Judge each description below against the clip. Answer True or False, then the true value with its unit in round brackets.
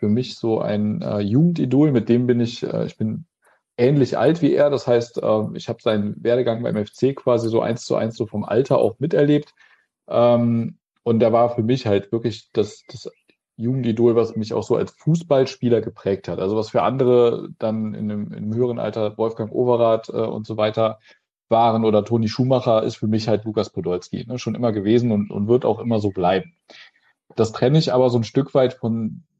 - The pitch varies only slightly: True (2.3 semitones)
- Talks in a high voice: False (115 Hz)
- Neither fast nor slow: False (210 wpm)